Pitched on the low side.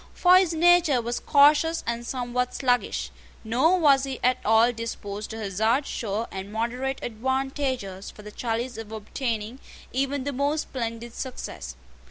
No: high, 245 Hz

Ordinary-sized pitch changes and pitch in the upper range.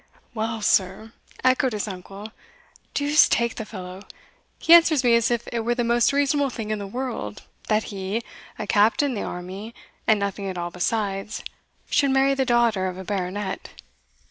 Yes: average, 3.9 semitones; high, 220 Hz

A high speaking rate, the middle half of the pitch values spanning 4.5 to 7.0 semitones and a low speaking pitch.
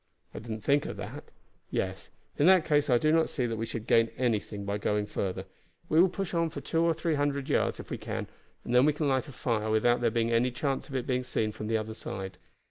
Yes: fast, 260 wpm; average, 5.2 semitones; low, 125 Hz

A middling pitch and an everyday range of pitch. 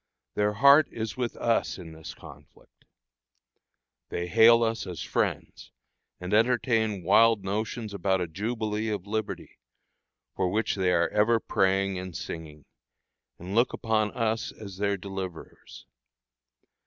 No: low, 105 Hz; average, 3.3 semitones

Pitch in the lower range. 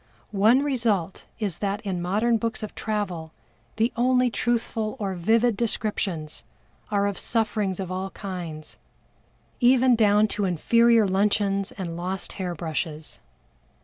No: high, 205 Hz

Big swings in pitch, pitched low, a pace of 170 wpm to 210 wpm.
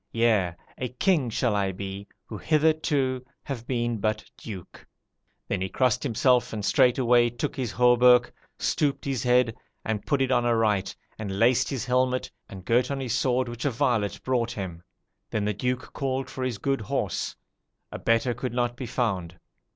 No: average, 3.0 semitones; low, 120 Hz; average, 175 wpm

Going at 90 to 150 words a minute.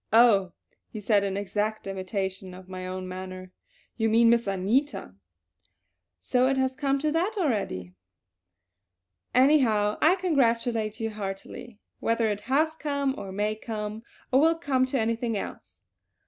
Yes: average, 145 wpm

